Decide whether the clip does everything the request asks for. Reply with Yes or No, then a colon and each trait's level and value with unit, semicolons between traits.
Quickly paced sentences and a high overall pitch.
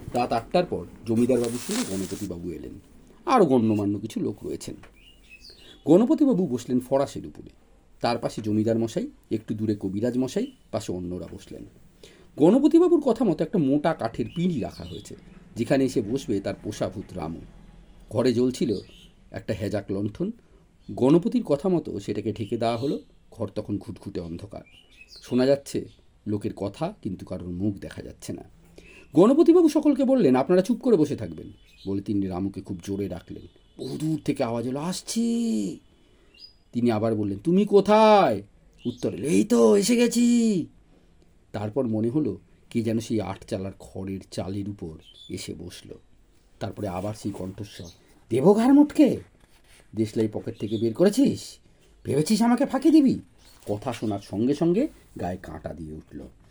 No: fast, 140 wpm; low, 115 Hz